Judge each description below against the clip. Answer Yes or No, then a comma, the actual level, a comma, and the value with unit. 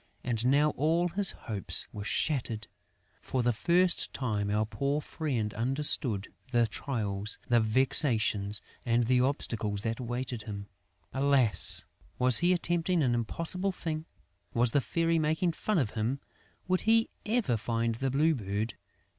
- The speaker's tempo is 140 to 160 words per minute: Yes, average, 145 wpm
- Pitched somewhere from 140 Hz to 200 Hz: No, low, 125 Hz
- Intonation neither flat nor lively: No, wide, 5.9 semitones